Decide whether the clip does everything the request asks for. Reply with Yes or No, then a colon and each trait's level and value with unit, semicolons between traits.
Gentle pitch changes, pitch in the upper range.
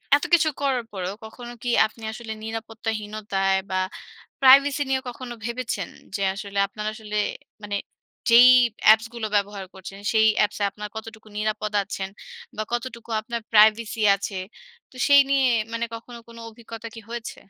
Yes: narrow, 2.2 semitones; high, 220 Hz